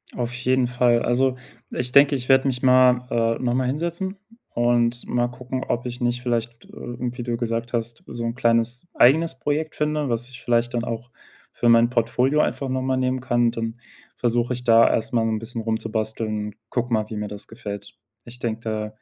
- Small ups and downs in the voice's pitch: Yes, narrow, 1.8 semitones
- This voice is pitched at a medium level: No, low, 120 Hz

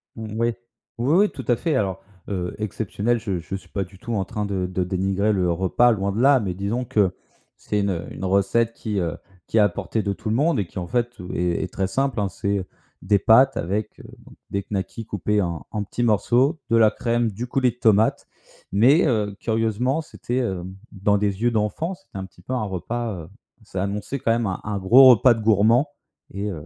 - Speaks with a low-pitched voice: Yes, low, 105 Hz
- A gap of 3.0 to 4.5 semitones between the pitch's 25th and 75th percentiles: Yes, average, 3.6 semitones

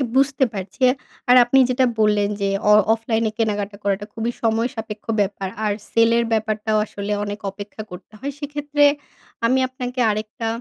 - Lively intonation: No, average, 3.1 semitones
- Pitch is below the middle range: No, high, 220 Hz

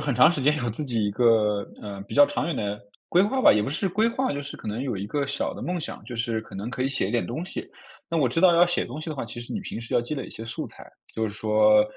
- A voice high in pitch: No, low, 125 Hz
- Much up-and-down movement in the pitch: Yes, wide, 6.2 semitones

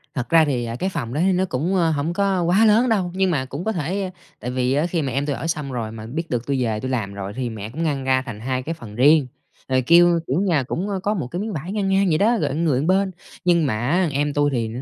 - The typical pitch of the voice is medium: Yes, medium, 150 Hz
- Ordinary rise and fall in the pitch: No, wide, 5.9 semitones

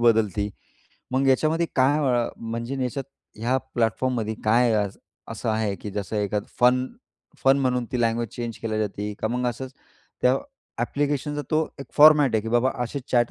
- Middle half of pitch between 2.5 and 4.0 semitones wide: Yes, average, 3.1 semitones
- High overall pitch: No, low, 120 Hz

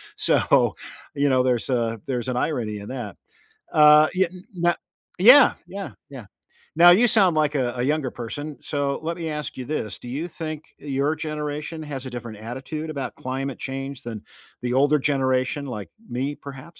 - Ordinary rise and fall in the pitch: Yes, average, 3.5 semitones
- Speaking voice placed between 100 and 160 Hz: Yes, medium, 140 Hz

